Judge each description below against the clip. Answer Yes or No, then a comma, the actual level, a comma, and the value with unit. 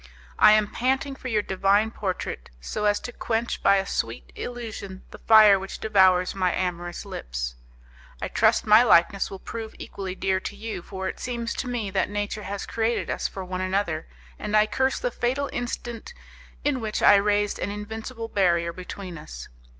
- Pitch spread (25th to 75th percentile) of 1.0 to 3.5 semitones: Yes, average, 3.2 semitones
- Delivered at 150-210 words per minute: Yes, average, 180 wpm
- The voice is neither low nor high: No, high, 205 Hz